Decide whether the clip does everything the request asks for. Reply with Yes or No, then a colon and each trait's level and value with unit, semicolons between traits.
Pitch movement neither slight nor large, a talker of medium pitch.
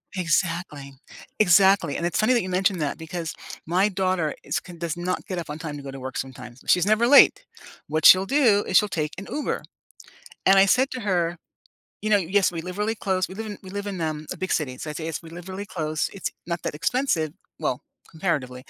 Yes: average, 4.0 semitones; medium, 180 Hz